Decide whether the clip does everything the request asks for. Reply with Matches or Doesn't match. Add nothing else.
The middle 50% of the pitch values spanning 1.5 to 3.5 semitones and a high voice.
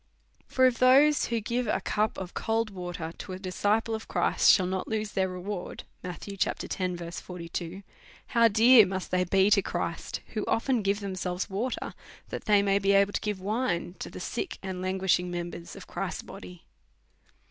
Matches